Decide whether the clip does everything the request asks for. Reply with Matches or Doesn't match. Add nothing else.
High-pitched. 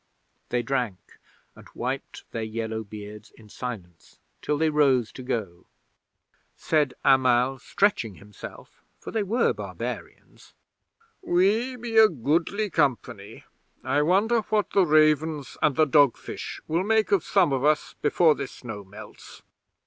Doesn't match